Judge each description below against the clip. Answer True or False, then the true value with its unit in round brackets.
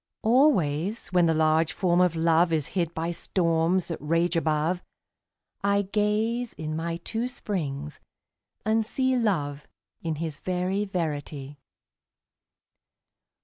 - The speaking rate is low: True (120 wpm)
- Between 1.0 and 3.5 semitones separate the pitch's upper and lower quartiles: False (4.3 semitones)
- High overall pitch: False (170 Hz)